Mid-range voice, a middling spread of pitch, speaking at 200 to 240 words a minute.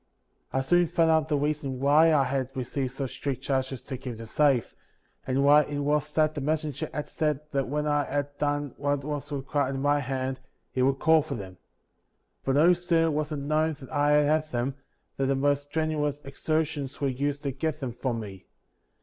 No: medium, 145 Hz; narrow, 2.1 semitones; fast, 205 wpm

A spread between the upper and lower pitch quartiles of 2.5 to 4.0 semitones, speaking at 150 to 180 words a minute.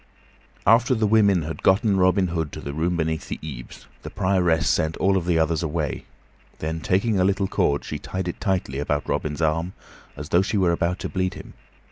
No: average, 3.3 semitones; fast, 205 wpm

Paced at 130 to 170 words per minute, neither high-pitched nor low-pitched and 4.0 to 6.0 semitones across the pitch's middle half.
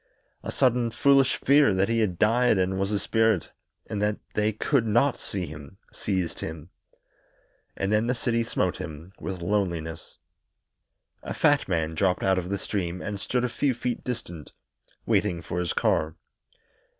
No: average, 165 wpm; low, 100 Hz; average, 4.8 semitones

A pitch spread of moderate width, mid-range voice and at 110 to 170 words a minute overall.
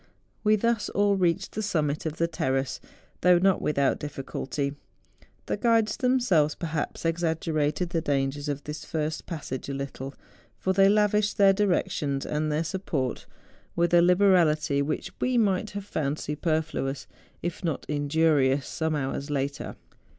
Yes: average, 4.8 semitones; medium, 160 Hz; average, 150 wpm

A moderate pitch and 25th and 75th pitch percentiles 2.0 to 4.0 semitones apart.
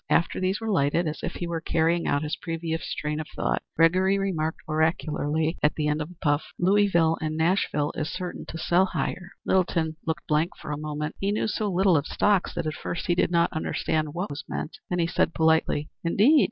Yes: medium, 165 Hz; narrow, 2.6 semitones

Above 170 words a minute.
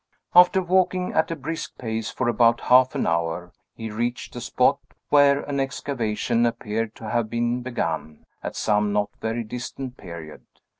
No: average, 160 wpm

